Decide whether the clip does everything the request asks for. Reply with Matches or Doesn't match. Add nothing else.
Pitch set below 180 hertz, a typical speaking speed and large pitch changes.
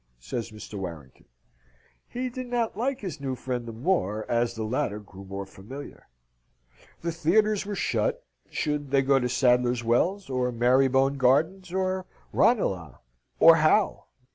Matches